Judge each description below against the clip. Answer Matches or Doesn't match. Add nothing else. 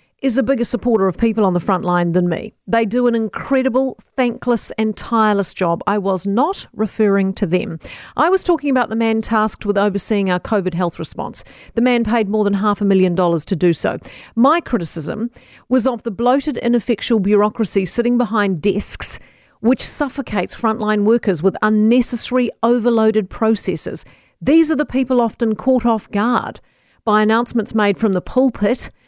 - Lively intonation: Doesn't match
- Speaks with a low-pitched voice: Doesn't match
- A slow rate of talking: Doesn't match